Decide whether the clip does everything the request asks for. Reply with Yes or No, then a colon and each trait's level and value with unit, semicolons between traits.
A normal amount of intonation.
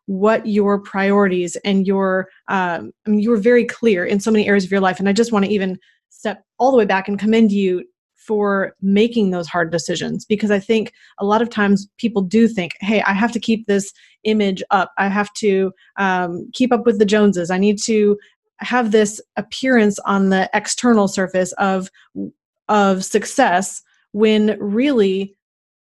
No: narrow, 2.2 semitones